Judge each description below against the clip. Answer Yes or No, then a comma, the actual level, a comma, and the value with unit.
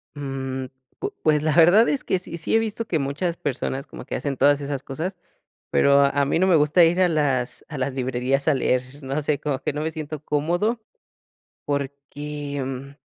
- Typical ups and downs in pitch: Yes, average, 3.1 semitones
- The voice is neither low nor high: Yes, medium, 145 Hz